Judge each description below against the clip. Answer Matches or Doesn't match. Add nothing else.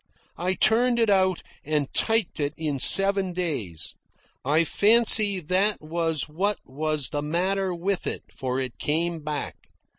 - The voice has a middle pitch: Matches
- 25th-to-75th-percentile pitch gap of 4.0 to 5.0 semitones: Matches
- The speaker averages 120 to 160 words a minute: Matches